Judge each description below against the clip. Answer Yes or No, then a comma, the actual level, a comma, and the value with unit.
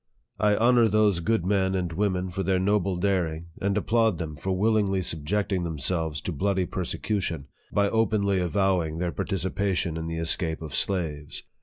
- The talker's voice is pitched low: Yes, very low, 95 Hz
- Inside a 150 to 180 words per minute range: Yes, average, 170 wpm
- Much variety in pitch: No, average, 3.4 semitones